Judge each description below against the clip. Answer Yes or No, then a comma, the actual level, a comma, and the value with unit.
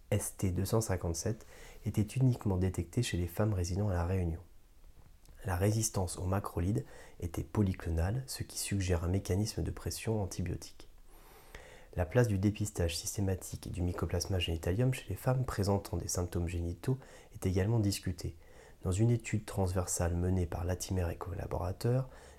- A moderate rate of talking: No, slow, 140 wpm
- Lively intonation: No, average, 3.5 semitones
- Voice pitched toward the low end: Yes, very low, 95 Hz